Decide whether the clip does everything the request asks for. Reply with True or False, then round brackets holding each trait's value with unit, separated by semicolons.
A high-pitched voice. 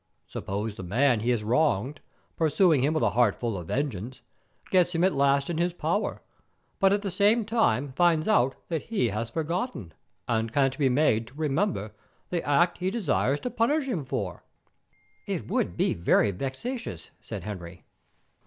False (140 Hz)